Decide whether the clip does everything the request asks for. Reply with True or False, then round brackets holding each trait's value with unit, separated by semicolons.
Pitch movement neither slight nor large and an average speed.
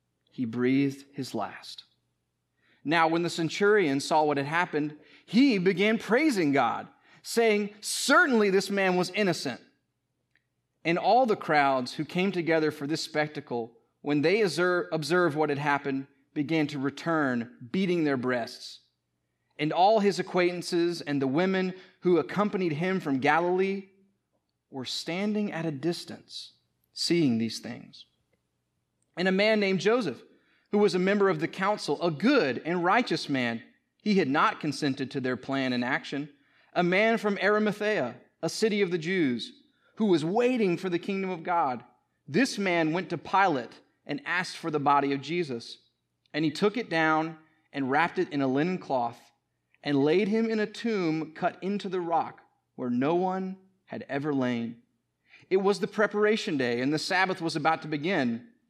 False (5.8 semitones; 165 wpm)